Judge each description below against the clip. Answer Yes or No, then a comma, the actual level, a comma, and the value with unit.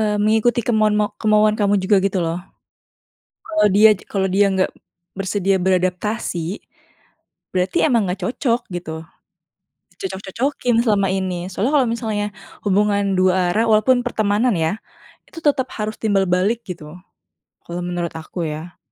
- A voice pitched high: Yes, high, 200 Hz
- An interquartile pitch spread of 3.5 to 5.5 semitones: No, average, 3.1 semitones